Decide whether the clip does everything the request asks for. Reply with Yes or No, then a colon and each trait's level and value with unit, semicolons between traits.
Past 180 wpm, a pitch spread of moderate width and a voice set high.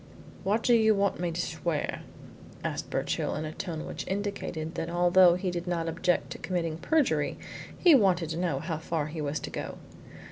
No: average, 190 wpm; average, 3.0 semitones; medium, 175 Hz